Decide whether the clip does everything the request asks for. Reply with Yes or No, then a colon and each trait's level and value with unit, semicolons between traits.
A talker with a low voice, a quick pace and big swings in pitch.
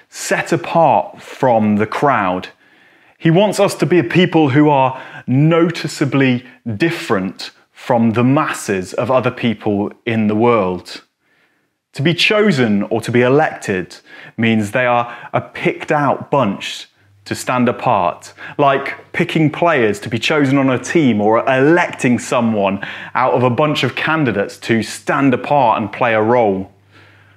No: low, 125 Hz; average, 145 wpm; wide, 5.7 semitones